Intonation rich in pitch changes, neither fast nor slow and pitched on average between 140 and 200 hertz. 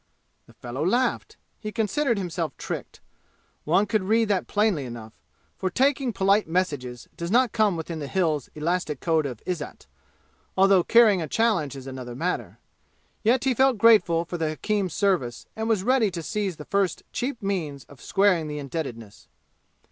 Yes: wide, 5.9 semitones; average, 165 wpm; medium, 185 Hz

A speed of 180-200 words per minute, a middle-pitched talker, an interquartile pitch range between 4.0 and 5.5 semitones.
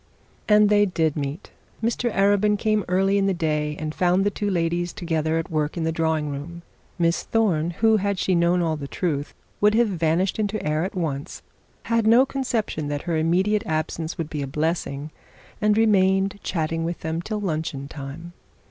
Yes: average, 185 wpm; medium, 170 Hz; average, 4.4 semitones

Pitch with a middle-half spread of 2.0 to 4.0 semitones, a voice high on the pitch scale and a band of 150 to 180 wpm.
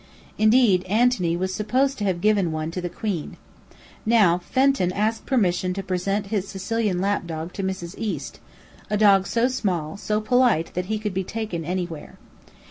Yes: average, 3.3 semitones; high, 195 Hz; average, 170 wpm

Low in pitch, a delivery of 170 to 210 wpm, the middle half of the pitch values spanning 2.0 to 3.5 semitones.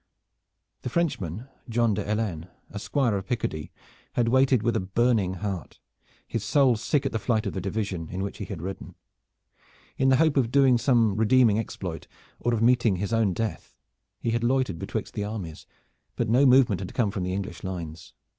No: low, 110 Hz; average, 190 wpm; average, 4.1 semitones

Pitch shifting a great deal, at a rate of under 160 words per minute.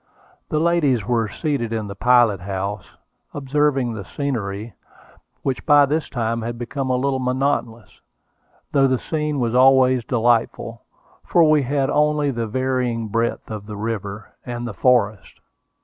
No: average, 3.7 semitones; average, 150 wpm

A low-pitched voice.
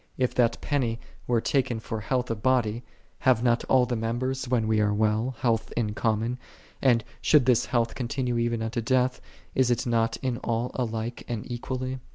Yes: low, 120 Hz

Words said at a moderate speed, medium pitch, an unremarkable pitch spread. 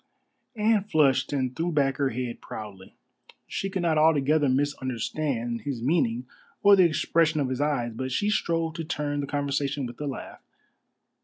Yes: average, 165 wpm; medium, 145 Hz; average, 3.9 semitones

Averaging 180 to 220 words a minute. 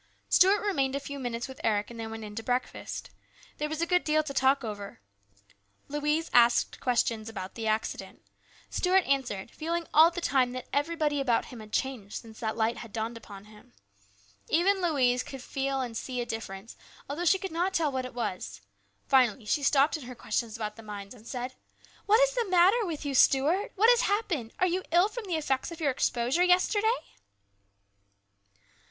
Yes: average, 195 wpm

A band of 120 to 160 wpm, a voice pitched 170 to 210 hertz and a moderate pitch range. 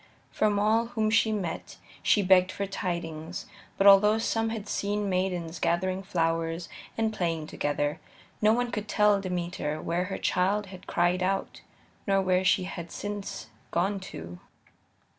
Yes: average, 150 wpm; high, 190 Hz; average, 3.2 semitones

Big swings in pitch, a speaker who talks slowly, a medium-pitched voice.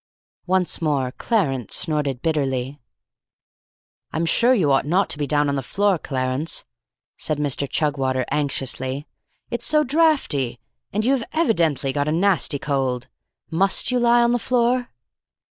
No: wide, 7.2 semitones; average, 150 wpm; medium, 150 Hz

